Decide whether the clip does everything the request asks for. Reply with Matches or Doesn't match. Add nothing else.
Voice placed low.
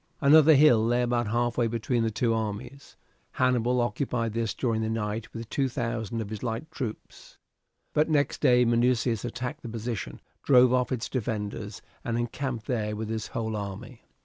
Matches